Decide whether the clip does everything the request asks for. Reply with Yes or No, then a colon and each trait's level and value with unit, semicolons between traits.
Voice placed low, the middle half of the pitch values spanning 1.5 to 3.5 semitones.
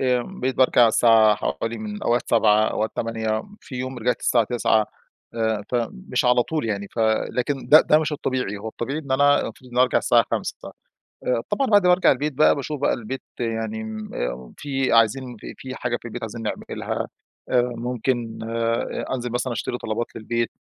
Yes: low, 120 Hz; average, 2.8 semitones